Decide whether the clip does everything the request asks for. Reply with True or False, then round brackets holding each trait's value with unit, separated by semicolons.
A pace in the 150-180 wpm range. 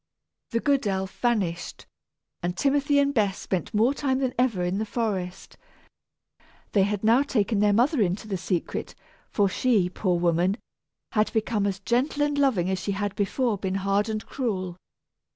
True (170 wpm)